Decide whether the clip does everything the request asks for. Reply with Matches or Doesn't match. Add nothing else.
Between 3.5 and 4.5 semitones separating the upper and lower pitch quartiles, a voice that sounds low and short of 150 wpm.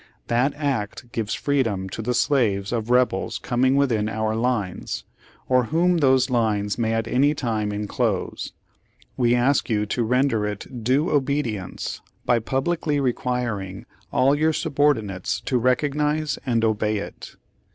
Matches